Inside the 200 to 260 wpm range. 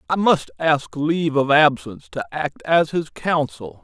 No: average, 170 wpm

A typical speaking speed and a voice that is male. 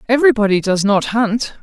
No: average, 185 wpm; female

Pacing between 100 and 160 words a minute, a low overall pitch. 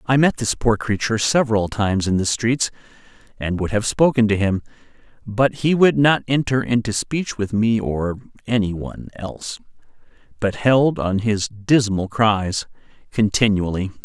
Yes: average, 155 wpm; low, 110 Hz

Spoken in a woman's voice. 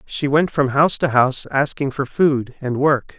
No: male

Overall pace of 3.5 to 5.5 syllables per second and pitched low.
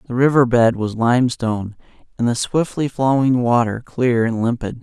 Yes: 5.0 syllables/s; low, 120 Hz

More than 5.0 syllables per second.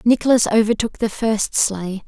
No: 4.7 syllables/s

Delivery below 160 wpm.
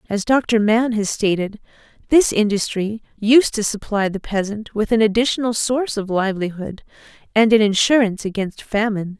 Yes: average, 150 wpm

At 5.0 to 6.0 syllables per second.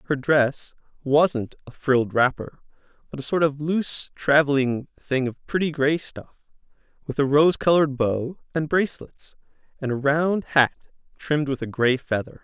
No: 4.6 syllables/s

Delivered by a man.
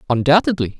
Yes: male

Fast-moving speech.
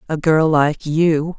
No: average, 175 wpm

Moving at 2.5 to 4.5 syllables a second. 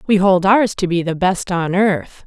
Yes: 4.3 syllables/s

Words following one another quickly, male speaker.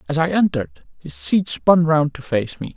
Yes: fast, 215 wpm; male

